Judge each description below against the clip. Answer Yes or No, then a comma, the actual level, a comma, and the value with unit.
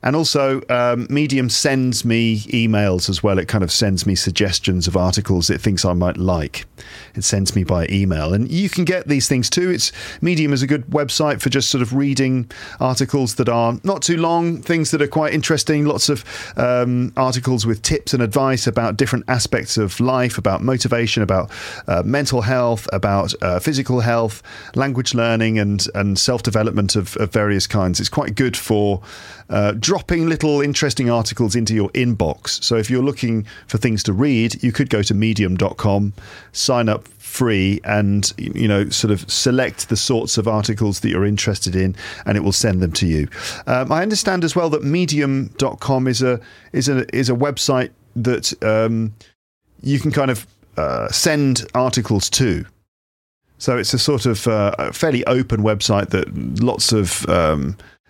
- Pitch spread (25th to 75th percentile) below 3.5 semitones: No, average, 4.5 semitones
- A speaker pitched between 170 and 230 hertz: No, low, 115 Hz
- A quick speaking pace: No, average, 180 wpm